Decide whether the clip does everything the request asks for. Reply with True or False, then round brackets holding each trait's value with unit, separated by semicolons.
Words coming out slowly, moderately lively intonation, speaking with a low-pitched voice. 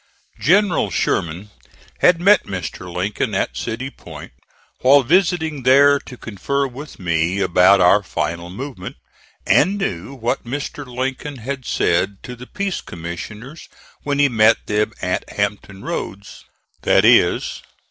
False (130 wpm; 6.9 semitones; 120 Hz)